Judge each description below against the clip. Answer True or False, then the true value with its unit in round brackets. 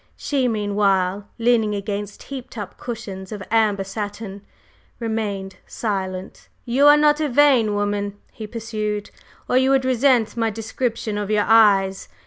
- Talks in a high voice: True (215 Hz)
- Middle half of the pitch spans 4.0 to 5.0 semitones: False (2.9 semitones)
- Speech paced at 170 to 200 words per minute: False (140 wpm)